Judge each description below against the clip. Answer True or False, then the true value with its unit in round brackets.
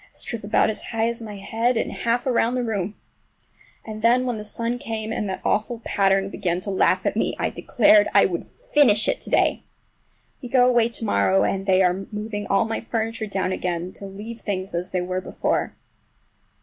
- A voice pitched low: False (215 Hz)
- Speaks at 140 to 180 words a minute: False (205 wpm)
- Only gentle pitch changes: False (3.3 semitones)